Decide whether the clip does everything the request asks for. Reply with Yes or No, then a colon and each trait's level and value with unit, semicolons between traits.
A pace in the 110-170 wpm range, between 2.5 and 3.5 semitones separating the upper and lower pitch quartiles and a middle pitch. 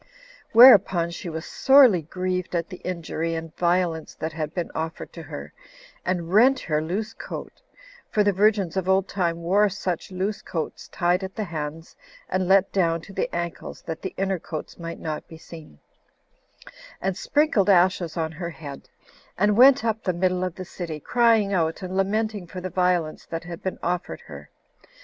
No: average, 180 wpm; average, 2.8 semitones; medium, 180 Hz